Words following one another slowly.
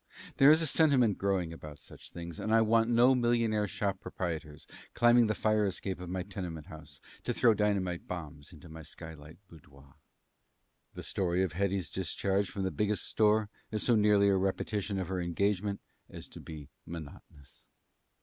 No: average, 170 wpm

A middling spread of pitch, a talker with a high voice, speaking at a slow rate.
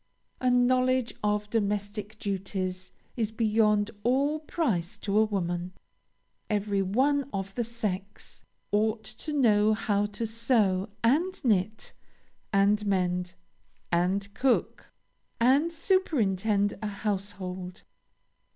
Yes: average, 3.3 semitones; high, 210 Hz; slow, 105 wpm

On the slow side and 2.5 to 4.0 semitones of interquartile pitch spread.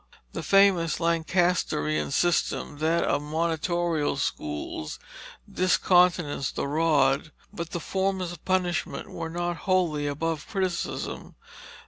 Yes: slow, 105 wpm; average, 3.2 semitones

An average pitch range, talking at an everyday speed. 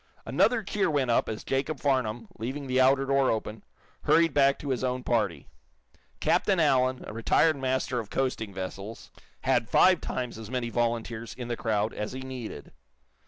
Yes: average, 3.3 semitones; average, 170 wpm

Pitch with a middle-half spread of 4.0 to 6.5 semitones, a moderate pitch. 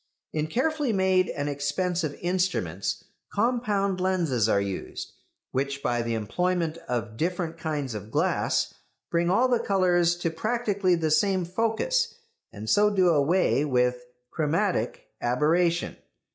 Yes: average, 5.3 semitones; medium, 170 Hz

